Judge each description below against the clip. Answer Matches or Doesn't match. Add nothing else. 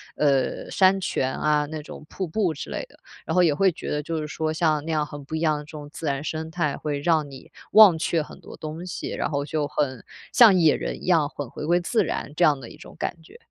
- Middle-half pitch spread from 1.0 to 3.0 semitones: Matches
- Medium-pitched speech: Matches